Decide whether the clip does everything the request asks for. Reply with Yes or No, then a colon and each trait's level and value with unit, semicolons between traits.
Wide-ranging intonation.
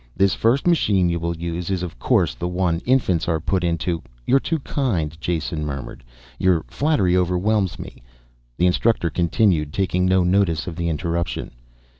No: average, 2.7 semitones